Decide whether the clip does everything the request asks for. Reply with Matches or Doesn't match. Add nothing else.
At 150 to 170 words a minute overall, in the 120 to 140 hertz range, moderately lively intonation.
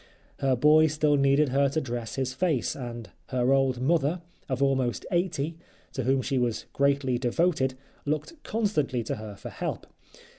Matches